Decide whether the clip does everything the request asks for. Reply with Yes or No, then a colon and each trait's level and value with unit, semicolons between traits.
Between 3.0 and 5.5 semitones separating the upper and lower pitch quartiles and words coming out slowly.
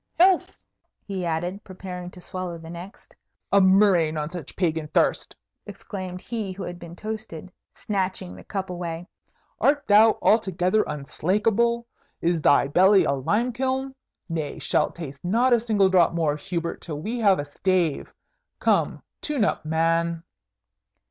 No: average, 4.0 semitones; average, 150 wpm